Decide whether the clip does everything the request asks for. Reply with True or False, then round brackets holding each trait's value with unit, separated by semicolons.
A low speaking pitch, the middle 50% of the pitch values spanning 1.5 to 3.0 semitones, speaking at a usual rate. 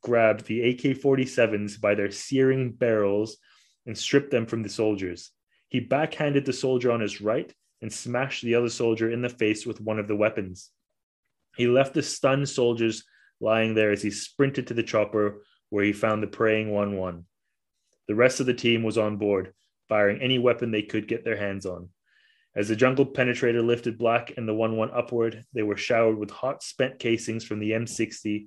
True (115 Hz; 2.7 semitones; 195 wpm)